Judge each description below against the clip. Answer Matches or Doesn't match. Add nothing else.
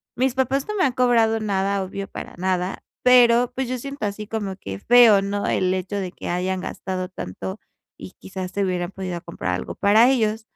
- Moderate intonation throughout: Matches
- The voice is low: Doesn't match